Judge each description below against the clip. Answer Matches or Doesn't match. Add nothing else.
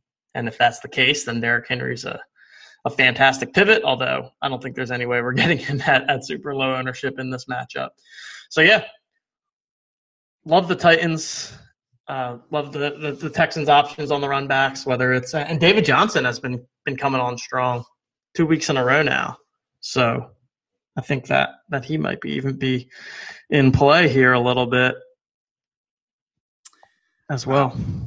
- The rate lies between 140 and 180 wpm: Matches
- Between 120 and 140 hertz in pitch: Matches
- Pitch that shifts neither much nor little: Matches